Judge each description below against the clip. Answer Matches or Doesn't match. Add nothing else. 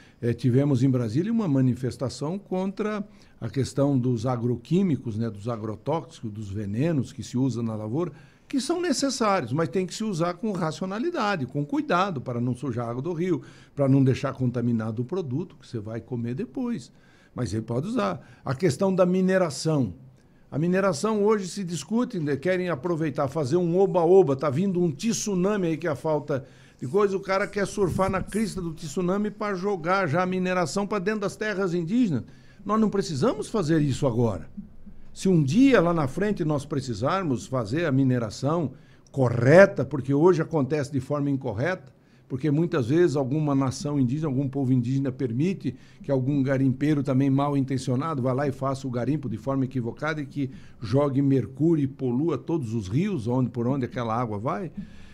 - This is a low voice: Doesn't match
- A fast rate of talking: Doesn't match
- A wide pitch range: Matches